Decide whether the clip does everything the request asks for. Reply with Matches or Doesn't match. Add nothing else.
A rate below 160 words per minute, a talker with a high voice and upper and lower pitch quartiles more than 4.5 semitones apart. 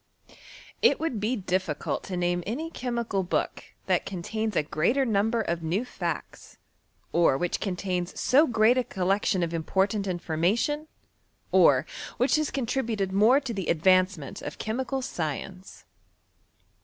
Matches